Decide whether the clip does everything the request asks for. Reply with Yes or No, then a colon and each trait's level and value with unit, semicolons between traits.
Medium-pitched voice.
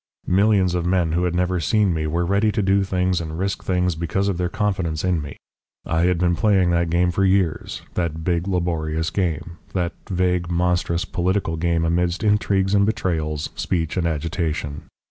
No: very low, 90 Hz